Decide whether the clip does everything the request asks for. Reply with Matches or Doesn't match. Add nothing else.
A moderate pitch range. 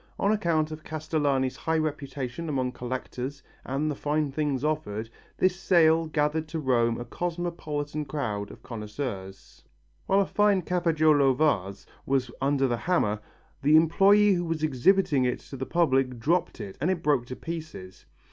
Matches